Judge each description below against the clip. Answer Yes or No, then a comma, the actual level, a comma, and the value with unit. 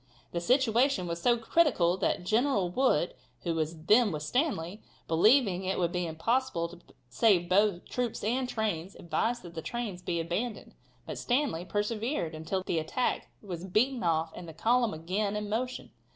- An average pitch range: No, wide, 5.9 semitones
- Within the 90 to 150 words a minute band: No, average, 165 wpm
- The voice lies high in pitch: Yes, high, 195 Hz